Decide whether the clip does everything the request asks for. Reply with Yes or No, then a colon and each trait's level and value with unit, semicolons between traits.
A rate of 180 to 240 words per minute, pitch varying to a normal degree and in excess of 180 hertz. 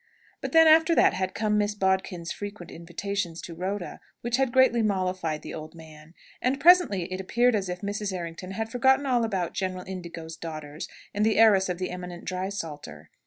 Yes: average, 185 wpm; average, 4.2 semitones; high, 190 Hz